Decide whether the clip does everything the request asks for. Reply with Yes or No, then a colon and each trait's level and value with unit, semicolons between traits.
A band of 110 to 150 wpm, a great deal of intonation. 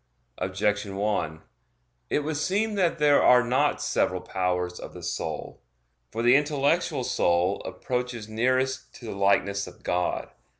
Yes: average, 140 wpm; wide, 6.4 semitones